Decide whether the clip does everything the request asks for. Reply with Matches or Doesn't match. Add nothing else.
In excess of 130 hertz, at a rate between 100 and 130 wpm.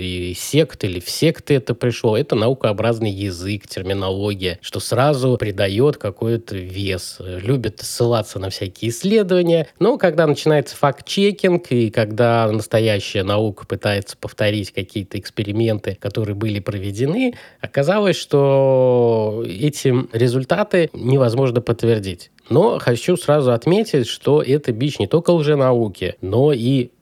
Doesn't match